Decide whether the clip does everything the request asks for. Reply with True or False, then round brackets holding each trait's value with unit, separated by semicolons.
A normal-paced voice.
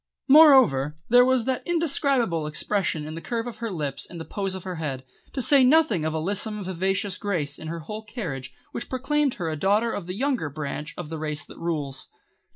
False (210 wpm)